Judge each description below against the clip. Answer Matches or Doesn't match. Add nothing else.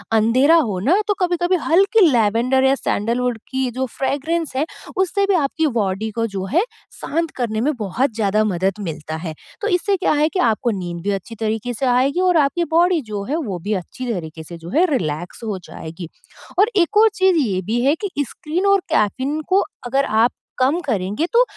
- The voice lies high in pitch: Matches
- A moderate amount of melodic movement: Doesn't match